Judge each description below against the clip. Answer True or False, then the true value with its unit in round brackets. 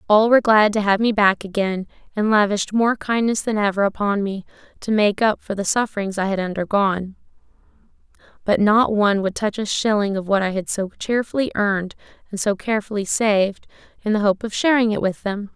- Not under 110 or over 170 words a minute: False (195 wpm)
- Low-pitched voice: False (205 Hz)